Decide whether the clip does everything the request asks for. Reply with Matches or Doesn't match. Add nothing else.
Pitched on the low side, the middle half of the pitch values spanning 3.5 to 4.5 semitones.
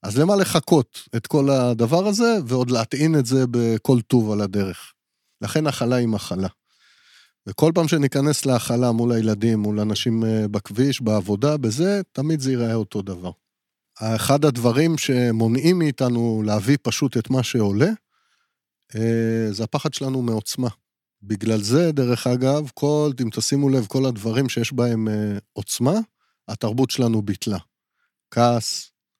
Matches